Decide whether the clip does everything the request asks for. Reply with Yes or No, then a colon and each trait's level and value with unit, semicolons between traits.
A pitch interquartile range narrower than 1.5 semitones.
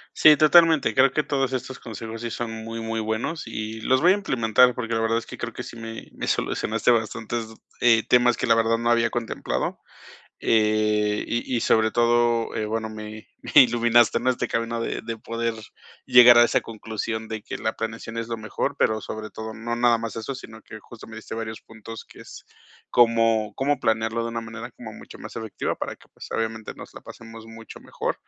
Yes: narrow, 1.1 semitones